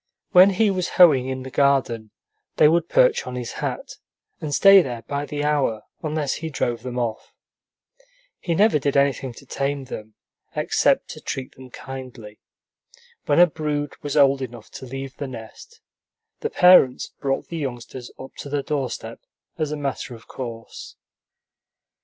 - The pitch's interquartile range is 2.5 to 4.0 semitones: Yes, average, 3.4 semitones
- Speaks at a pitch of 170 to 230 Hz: No, medium, 140 Hz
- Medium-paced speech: Yes, average, 165 wpm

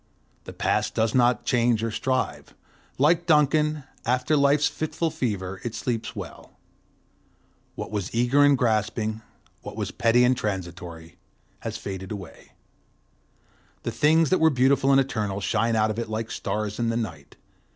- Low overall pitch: Yes, low, 115 Hz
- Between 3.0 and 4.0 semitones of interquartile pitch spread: No, average, 4.5 semitones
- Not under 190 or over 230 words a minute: No, average, 150 wpm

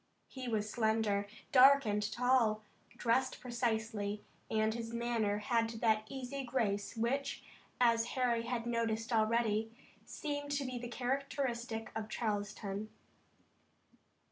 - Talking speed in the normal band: No, slow, 115 wpm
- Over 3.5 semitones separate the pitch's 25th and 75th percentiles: No, narrow, 2.5 semitones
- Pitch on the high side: Yes, high, 230 Hz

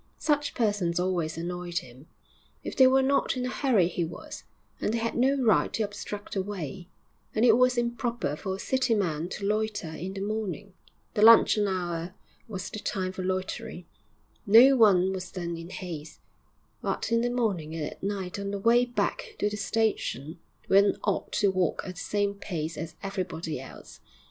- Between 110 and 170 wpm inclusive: No, average, 185 wpm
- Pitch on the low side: No, high, 200 Hz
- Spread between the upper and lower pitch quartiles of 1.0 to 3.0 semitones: No, average, 4.2 semitones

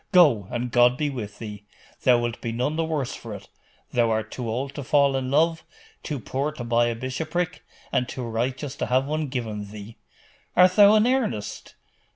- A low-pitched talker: Yes, low, 130 Hz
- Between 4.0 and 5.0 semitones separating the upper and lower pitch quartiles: Yes, average, 4.6 semitones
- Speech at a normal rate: Yes, average, 195 wpm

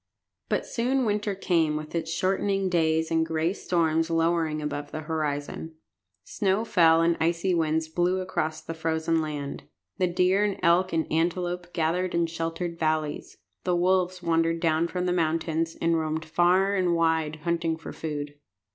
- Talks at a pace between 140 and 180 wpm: Yes, average, 160 wpm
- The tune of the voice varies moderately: No, narrow, 2.0 semitones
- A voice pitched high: No, medium, 165 Hz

